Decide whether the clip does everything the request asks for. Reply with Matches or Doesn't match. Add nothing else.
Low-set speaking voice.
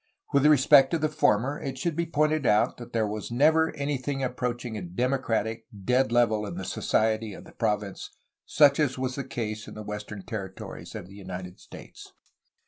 Matches